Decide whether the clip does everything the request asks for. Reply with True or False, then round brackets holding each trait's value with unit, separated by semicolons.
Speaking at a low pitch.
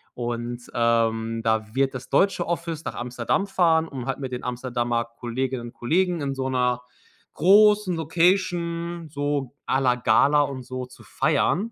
True (130 Hz)